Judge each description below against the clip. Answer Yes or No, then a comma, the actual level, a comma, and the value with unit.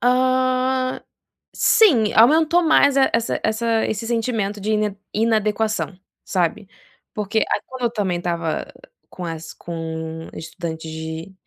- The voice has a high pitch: Yes, high, 215 Hz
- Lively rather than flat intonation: Yes, wide, 6.2 semitones